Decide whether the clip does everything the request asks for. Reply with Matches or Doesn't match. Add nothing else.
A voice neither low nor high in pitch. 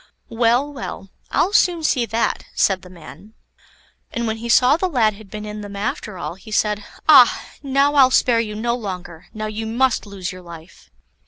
Doesn't match